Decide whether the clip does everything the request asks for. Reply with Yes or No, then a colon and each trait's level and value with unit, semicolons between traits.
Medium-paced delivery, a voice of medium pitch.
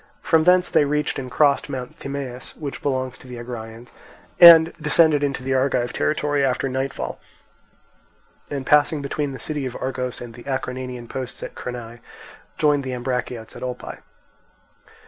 No: average, 155 wpm; low, 130 Hz